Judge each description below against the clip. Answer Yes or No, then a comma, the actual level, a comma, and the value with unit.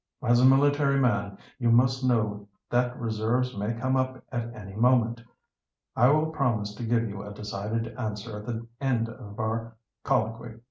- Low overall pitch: Yes, low, 115 Hz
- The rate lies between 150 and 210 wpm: Yes, average, 170 wpm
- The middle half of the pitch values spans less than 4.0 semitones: Yes, average, 2.8 semitones